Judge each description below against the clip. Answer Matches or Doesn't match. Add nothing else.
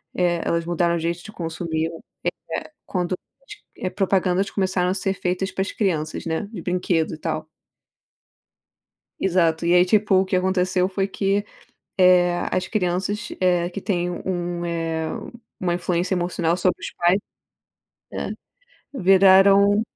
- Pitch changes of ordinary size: Doesn't match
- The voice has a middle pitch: Matches